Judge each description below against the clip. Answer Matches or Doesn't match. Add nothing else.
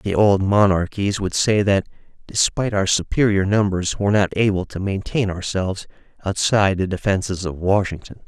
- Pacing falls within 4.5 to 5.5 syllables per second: Matches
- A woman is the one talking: Doesn't match